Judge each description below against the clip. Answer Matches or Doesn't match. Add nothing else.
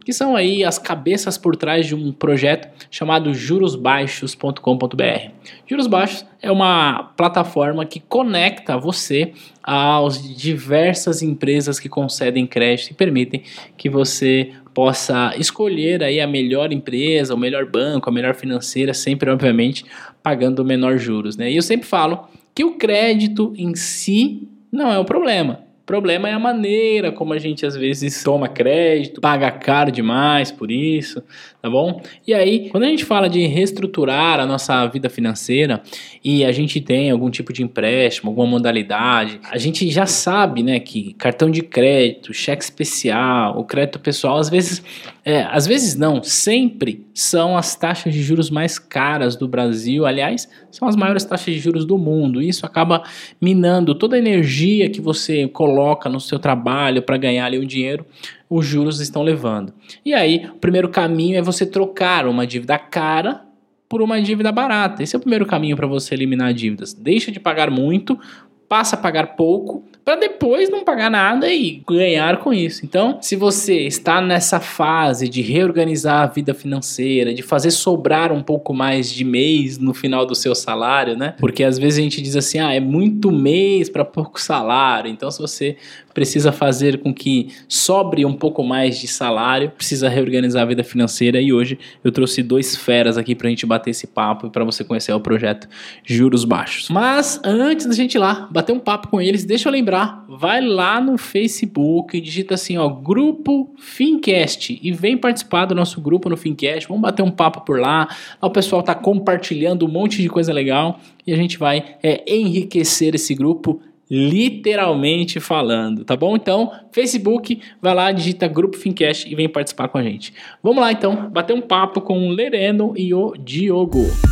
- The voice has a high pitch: Doesn't match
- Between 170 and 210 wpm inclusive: Matches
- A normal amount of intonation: Doesn't match